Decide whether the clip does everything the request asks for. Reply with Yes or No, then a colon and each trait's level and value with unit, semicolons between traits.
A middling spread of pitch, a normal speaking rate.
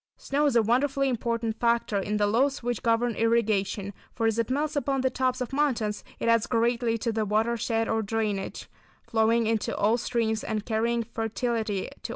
No: narrow, 1.8 semitones; average, 195 wpm